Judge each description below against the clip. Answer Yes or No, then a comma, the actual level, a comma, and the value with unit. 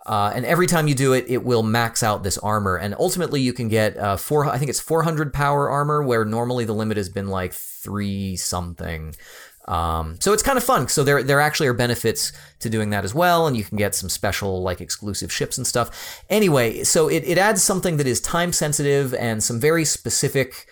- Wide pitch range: Yes, wide, 6.4 semitones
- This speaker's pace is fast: Yes, fast, 225 wpm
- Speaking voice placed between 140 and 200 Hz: No, low, 120 Hz